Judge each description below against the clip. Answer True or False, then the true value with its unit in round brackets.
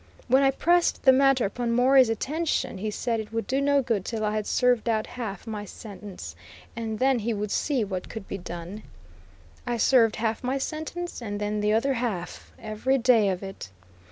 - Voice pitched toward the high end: True (225 Hz)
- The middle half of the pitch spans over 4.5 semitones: False (3.8 semitones)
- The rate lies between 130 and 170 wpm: False (195 wpm)